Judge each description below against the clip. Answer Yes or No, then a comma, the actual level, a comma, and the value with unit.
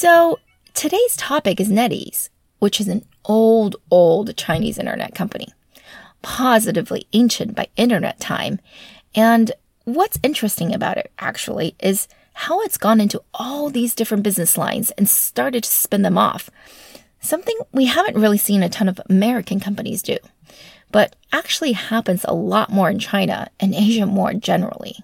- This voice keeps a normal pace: Yes, average, 150 wpm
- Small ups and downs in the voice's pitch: No, average, 3.3 semitones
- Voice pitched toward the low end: No, high, 220 Hz